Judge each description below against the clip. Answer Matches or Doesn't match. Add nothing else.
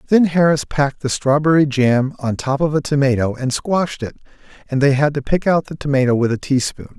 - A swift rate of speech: Matches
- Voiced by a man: Matches